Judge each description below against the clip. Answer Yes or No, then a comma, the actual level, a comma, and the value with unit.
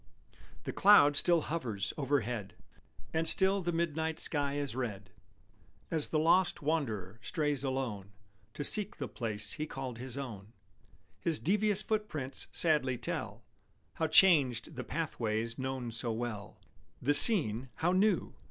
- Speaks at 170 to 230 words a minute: No, slow, 135 wpm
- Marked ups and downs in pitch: Yes, wide, 5.9 semitones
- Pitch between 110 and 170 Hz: Yes, medium, 140 Hz